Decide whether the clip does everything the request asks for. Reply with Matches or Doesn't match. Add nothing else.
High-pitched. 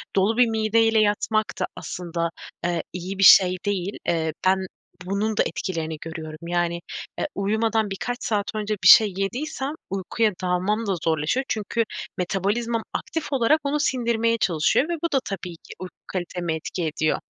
Matches